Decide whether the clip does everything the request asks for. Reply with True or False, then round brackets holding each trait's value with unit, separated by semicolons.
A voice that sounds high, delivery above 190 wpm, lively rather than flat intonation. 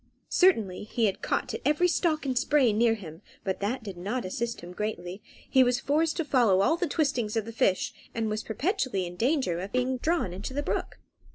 True (230 Hz; 205 wpm; 6.3 semitones)